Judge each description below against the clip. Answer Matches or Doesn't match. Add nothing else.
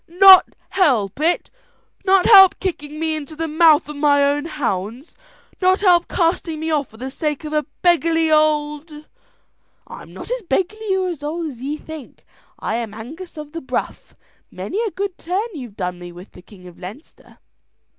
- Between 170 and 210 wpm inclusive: Matches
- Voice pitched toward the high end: Matches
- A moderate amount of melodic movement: Matches